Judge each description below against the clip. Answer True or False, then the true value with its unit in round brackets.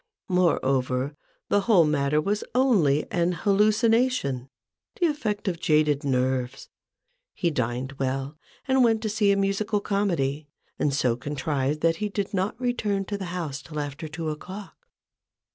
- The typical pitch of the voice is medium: True (170 Hz)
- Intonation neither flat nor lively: False (6.7 semitones)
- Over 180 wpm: False (145 wpm)